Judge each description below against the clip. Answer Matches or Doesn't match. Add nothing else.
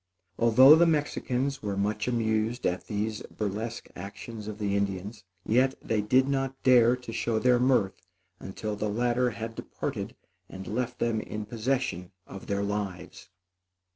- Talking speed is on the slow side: Doesn't match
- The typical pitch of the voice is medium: Doesn't match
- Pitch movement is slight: Doesn't match